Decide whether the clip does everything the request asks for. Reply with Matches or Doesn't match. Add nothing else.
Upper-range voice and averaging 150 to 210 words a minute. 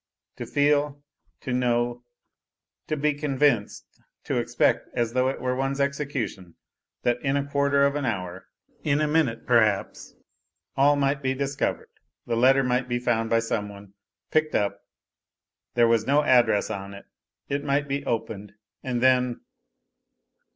Doesn't match